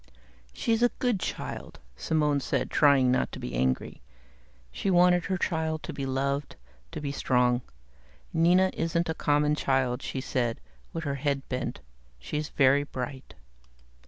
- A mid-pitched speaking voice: Yes, medium, 145 Hz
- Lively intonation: No, average, 3.8 semitones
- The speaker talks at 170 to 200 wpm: No, average, 150 wpm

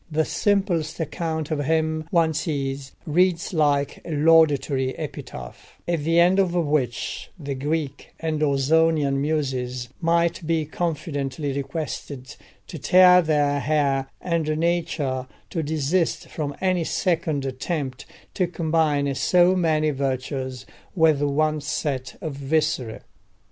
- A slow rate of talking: Yes, slow, 120 wpm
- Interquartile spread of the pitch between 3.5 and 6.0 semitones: No, average, 3.0 semitones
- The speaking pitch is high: No, medium, 155 Hz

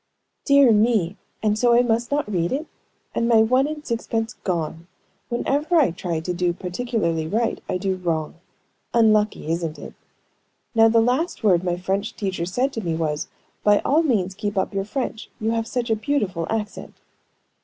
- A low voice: No, high, 215 Hz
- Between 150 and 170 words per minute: No, average, 180 wpm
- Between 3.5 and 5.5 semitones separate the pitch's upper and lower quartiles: Yes, average, 5.0 semitones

